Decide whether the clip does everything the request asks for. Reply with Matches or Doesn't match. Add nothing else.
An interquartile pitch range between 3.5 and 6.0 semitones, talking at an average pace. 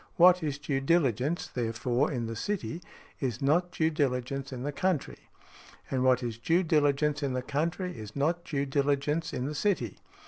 Matches